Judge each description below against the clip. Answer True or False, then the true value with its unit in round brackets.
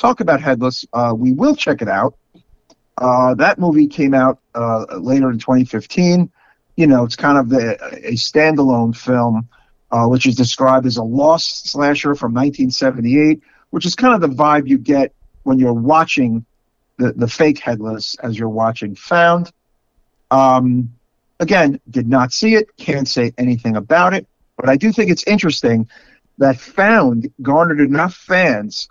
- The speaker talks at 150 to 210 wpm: True (160 wpm)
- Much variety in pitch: False (4.5 semitones)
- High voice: False (130 Hz)